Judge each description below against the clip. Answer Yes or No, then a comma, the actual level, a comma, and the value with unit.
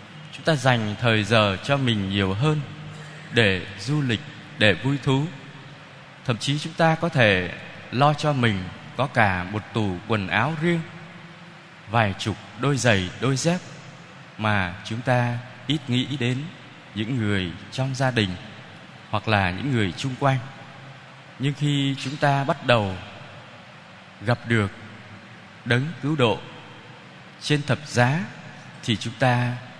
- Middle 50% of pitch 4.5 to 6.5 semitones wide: Yes, average, 5.3 semitones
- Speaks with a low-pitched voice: Yes, low, 125 Hz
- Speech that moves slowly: Yes, slow, 145 wpm